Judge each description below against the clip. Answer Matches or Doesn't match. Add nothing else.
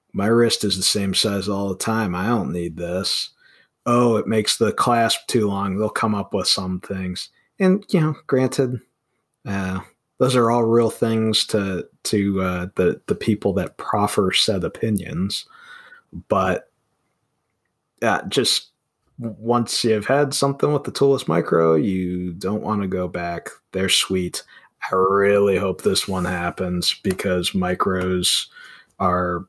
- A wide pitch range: Doesn't match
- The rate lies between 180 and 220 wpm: Doesn't match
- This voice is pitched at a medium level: Doesn't match